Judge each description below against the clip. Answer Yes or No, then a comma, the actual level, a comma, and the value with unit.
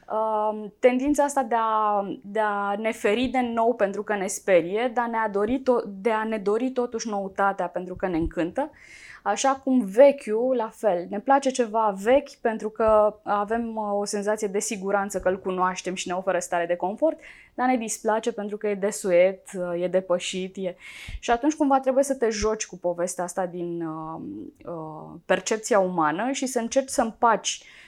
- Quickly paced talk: Yes, fast, 175 wpm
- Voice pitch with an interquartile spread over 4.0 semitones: Yes, average, 4.4 semitones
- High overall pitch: Yes, high, 215 Hz